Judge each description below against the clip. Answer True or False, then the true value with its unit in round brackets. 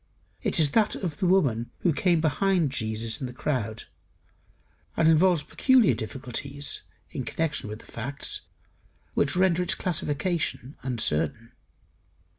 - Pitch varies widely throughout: True (6.7 semitones)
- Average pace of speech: False (130 wpm)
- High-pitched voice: False (145 Hz)